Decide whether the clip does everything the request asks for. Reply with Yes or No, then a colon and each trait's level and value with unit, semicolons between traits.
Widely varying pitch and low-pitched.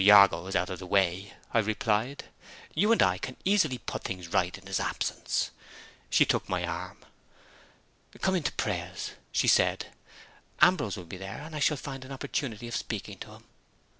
Yes: wide, 6.7 semitones; low, 100 Hz